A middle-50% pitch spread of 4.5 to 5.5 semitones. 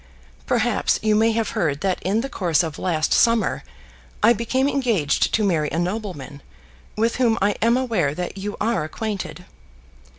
Yes: average, 4.9 semitones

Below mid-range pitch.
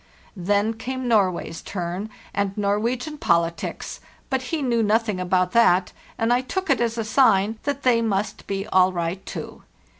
No: high, 210 Hz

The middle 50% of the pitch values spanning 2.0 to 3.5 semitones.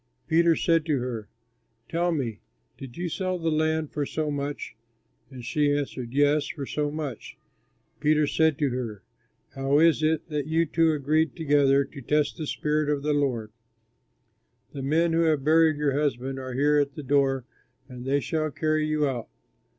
Yes: narrow, 2.5 semitones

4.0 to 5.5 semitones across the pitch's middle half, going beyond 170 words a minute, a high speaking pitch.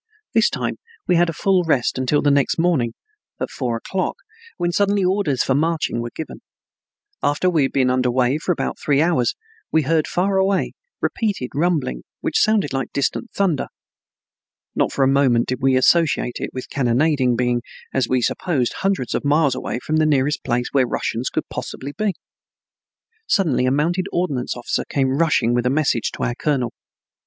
No: average, 5.1 semitones; average, 180 wpm; medium, 140 Hz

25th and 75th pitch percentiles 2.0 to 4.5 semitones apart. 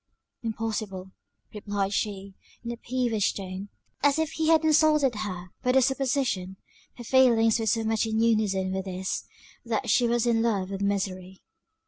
Yes: average, 4.1 semitones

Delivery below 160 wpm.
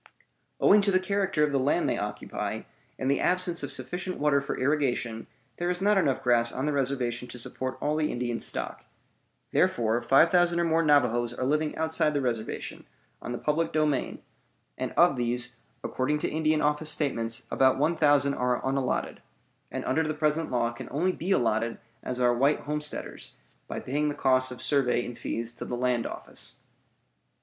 No: average, 180 wpm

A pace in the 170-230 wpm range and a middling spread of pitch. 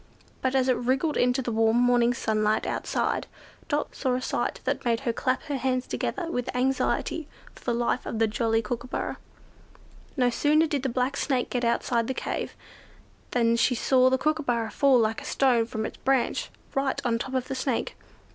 No: average, 190 wpm; narrow, 2.2 semitones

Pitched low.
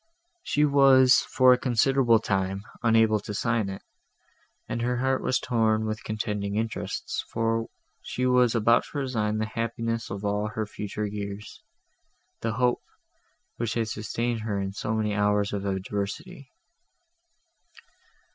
Yes: low, 110 Hz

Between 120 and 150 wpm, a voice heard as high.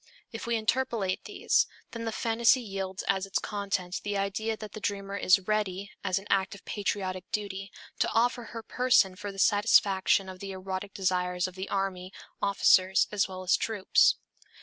No: average, 175 wpm; high, 195 Hz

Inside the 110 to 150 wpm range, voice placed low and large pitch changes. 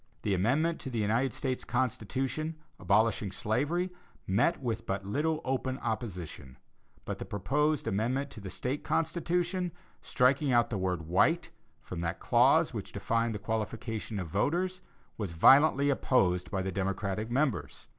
Yes: average, 145 wpm; low, 115 Hz; wide, 6.4 semitones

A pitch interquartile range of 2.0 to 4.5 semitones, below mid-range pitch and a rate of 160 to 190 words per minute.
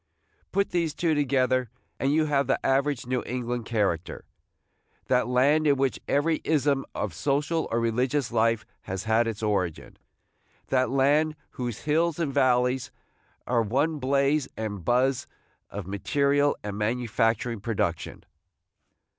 No: average, 3.9 semitones; low, 130 Hz; average, 140 wpm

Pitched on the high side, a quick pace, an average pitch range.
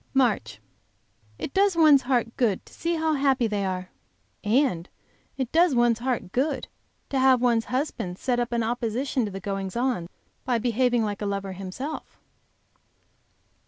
No: high, 240 Hz; average, 160 wpm; average, 4.6 semitones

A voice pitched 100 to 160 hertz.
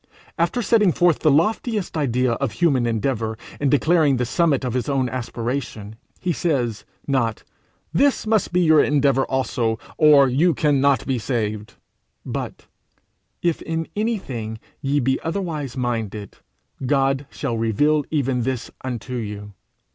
Yes: low, 135 Hz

